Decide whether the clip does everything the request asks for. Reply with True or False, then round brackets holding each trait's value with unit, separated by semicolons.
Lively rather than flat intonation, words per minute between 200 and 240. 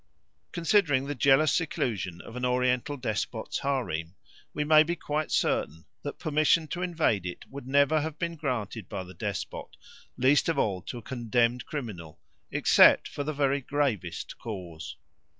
False (5.8 semitones; 155 wpm)